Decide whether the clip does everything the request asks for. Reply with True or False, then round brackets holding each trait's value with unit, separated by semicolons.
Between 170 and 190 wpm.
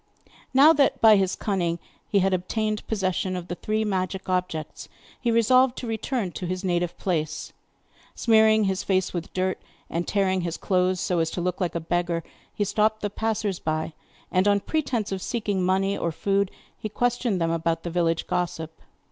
True (180 wpm)